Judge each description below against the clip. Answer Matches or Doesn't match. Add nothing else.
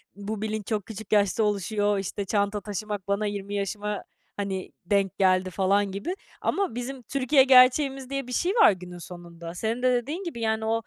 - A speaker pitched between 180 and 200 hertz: Doesn't match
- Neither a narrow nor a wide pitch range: Matches